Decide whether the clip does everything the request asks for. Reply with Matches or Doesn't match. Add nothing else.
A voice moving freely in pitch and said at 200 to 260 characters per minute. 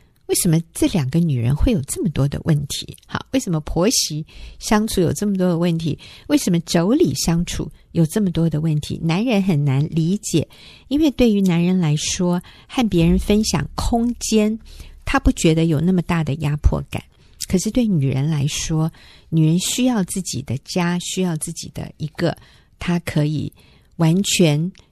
Doesn't match